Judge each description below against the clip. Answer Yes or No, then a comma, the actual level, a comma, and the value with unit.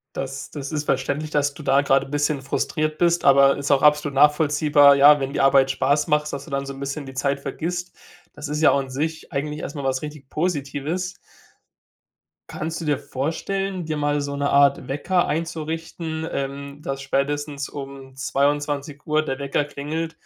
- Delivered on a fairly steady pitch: Yes, narrow, 1.9 semitones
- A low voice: No, medium, 145 Hz